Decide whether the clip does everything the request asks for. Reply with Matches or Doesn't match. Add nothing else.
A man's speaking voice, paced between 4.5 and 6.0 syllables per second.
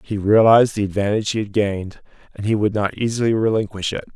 Doesn't match